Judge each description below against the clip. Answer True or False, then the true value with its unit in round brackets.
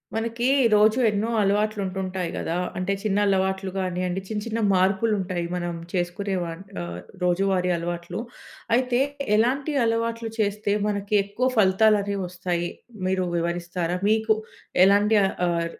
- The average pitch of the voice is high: True (195 Hz)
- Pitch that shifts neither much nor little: True (3.2 semitones)